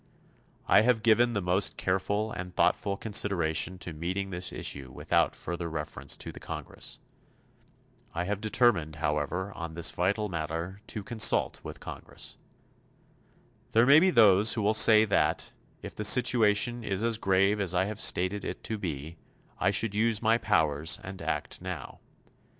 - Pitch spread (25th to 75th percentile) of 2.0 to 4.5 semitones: Yes, average, 4.0 semitones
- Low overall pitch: Yes, low, 100 Hz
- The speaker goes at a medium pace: Yes, average, 160 wpm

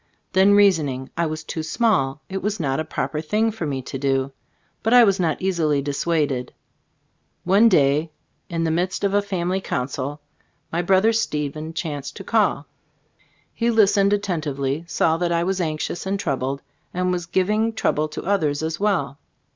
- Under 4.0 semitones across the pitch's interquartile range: No, average, 5.0 semitones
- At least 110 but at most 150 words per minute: No, average, 170 wpm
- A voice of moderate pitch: Yes, medium, 165 Hz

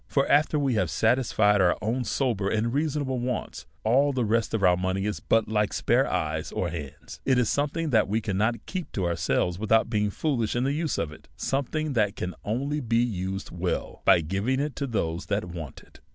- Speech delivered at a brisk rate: Yes, fast, 210 wpm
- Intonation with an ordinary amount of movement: No, wide, 5.8 semitones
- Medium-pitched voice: No, low, 110 Hz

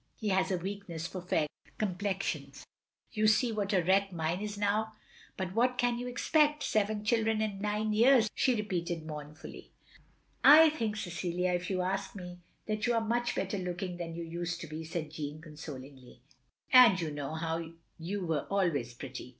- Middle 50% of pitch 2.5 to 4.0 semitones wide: No, average, 4.5 semitones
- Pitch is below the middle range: No, high, 190 Hz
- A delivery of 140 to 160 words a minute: No, average, 175 wpm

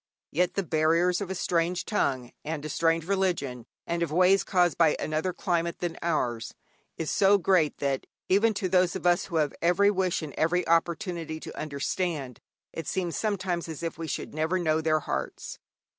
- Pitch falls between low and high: Yes, medium, 170 Hz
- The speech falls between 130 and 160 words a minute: No, average, 185 wpm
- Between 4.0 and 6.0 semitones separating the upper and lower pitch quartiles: No, average, 2.7 semitones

